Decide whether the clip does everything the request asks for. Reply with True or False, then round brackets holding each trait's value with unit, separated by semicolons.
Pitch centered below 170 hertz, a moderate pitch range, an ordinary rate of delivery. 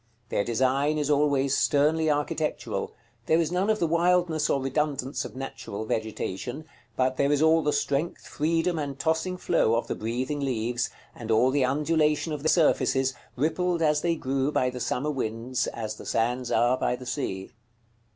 True (140 Hz; 3.8 semitones; 175 wpm)